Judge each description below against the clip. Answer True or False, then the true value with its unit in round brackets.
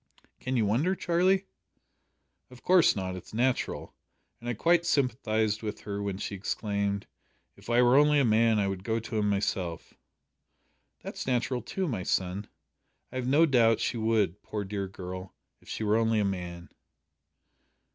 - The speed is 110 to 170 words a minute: True (165 wpm)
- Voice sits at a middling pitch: False (110 Hz)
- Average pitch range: True (4.1 semitones)